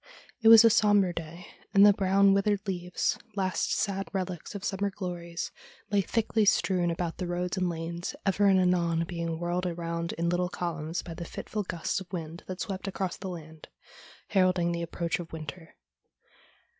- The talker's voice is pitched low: No, medium, 180 Hz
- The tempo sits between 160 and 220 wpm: Yes, average, 180 wpm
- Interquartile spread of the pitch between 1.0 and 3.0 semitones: Yes, narrow, 2.4 semitones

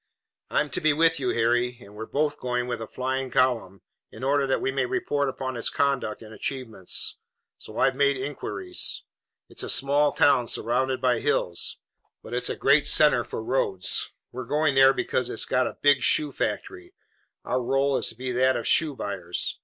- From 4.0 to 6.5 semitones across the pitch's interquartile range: No, average, 2.7 semitones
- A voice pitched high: No, low, 130 Hz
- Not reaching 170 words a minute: No, average, 190 wpm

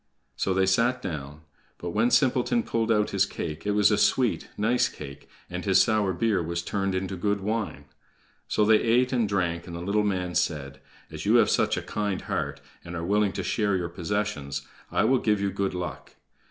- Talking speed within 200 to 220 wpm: Yes, fast, 205 wpm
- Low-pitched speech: Yes, low, 100 Hz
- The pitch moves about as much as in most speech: Yes, average, 3.7 semitones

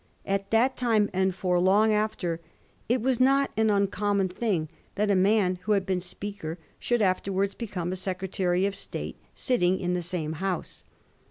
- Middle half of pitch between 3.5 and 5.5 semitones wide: No, average, 2.7 semitones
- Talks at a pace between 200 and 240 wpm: No, average, 170 wpm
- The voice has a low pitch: No, high, 195 Hz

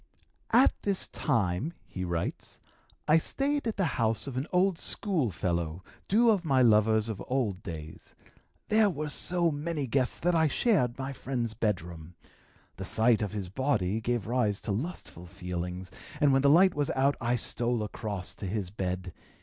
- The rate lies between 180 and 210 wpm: No, average, 170 wpm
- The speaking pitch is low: Yes, low, 120 Hz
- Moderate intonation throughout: No, wide, 7.7 semitones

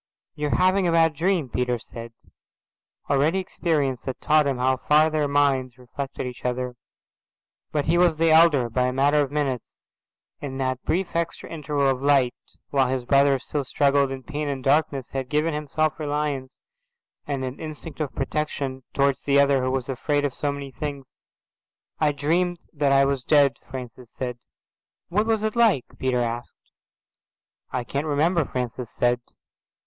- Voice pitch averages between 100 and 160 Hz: Yes, medium, 140 Hz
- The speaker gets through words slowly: No, average, 170 wpm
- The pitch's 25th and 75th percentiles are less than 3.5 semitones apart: Yes, average, 2.8 semitones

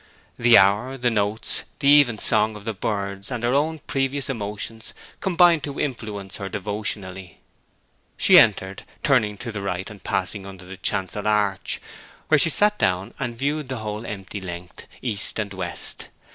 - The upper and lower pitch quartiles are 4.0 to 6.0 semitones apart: Yes, average, 4.8 semitones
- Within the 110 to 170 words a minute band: Yes, average, 165 wpm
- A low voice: Yes, low, 105 Hz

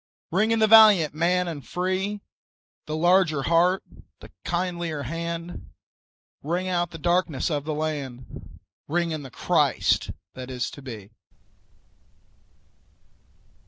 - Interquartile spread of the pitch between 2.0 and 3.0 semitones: No, average, 3.5 semitones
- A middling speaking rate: No, slow, 125 wpm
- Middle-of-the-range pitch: Yes, medium, 170 Hz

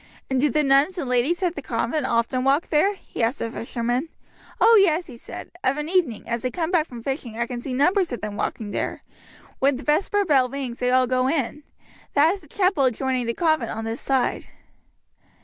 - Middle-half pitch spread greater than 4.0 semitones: Yes, average, 4.6 semitones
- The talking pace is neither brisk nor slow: No, fast, 220 wpm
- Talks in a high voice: Yes, very high, 270 Hz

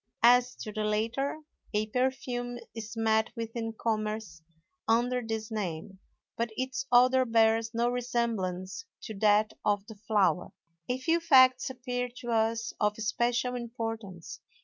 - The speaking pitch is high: Yes, high, 230 Hz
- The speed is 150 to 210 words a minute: No, average, 140 wpm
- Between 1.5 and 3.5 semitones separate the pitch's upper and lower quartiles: Yes, narrow, 2.5 semitones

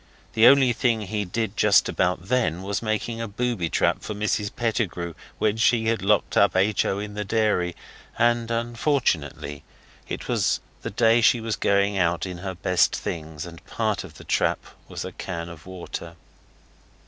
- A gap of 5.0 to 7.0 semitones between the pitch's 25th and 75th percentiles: No, average, 4.3 semitones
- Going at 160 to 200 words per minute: Yes, average, 175 wpm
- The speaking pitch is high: No, low, 105 Hz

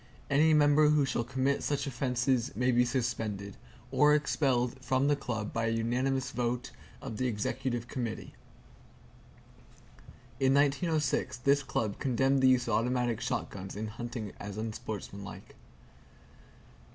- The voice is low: Yes, low, 125 Hz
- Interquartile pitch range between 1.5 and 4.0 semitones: Yes, average, 3.2 semitones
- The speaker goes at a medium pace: No, slow, 125 wpm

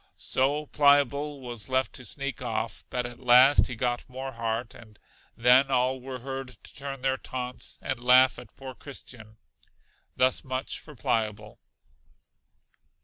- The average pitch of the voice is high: No, low, 130 Hz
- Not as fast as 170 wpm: Yes, average, 145 wpm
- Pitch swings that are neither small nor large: No, narrow, 1.8 semitones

